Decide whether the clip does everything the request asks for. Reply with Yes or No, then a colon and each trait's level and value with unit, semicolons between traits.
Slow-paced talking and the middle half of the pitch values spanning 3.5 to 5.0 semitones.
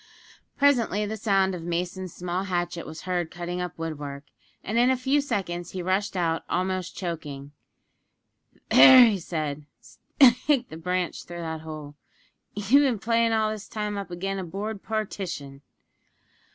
No: average, 150 wpm; average, 4.2 semitones